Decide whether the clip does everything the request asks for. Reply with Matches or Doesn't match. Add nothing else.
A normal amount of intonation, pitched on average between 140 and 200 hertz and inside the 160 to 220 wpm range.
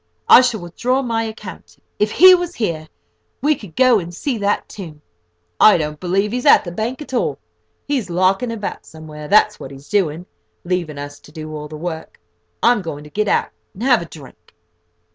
Doesn't match